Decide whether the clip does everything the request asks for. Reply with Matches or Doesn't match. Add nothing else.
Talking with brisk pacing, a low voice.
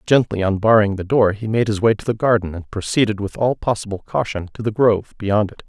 Matches